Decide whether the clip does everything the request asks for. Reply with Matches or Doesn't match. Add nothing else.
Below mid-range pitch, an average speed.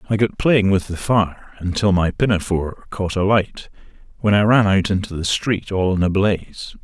Matches